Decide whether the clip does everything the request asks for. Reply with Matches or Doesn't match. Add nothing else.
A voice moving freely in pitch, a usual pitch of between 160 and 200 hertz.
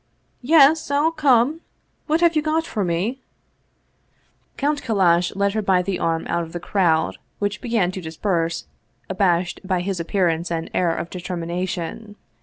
Matches